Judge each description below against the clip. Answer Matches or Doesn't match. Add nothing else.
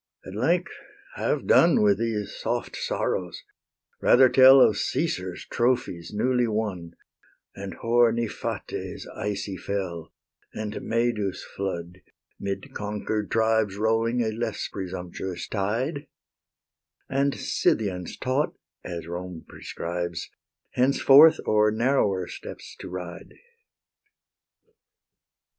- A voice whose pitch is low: Matches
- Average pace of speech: Doesn't match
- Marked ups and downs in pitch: Doesn't match